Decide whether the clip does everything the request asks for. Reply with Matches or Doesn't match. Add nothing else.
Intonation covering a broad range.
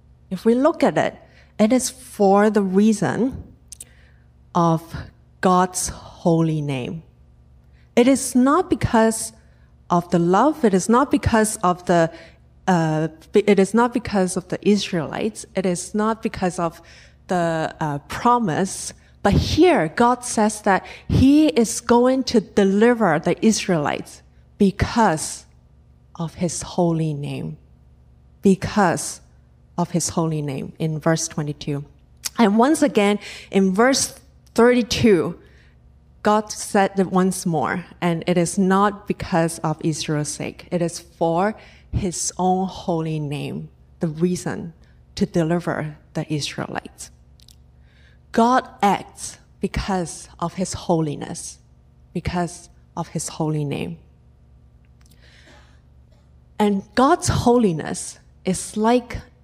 Matches